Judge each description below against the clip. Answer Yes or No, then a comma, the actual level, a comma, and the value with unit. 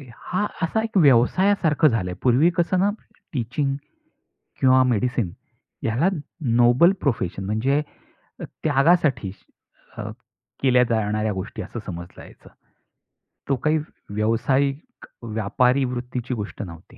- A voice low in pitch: Yes, low, 125 Hz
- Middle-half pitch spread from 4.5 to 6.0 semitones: Yes, average, 5.2 semitones